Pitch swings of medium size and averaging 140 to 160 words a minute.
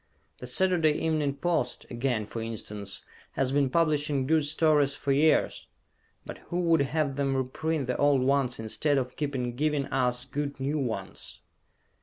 Yes: average, 3.2 semitones; average, 155 wpm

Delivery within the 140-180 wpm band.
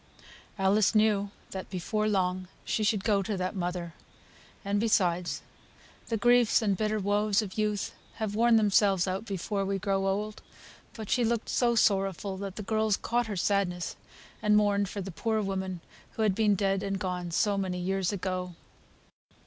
Yes: average, 170 wpm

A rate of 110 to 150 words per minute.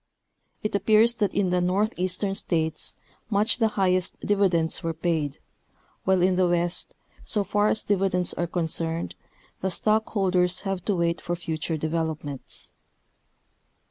Yes: average, 140 wpm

